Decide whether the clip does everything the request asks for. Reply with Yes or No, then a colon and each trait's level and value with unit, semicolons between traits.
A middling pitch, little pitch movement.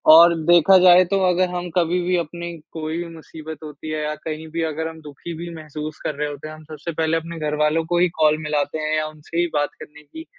Yes: medium, 160 Hz; narrow, 2.1 semitones